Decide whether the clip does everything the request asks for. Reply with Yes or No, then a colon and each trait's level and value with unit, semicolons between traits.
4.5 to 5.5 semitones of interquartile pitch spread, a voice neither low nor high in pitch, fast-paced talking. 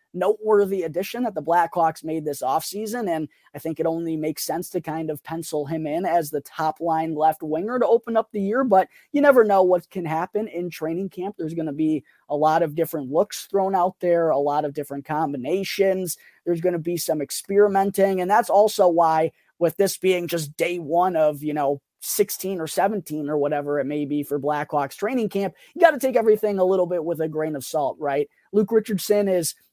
No: average, 3.9 semitones; medium, 170 Hz; fast, 215 wpm